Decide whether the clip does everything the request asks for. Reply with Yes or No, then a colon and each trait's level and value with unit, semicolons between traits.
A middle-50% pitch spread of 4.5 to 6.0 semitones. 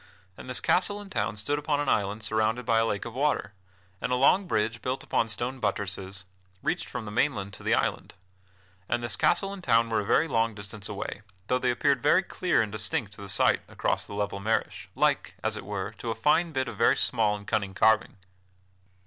No: average, 4.1 semitones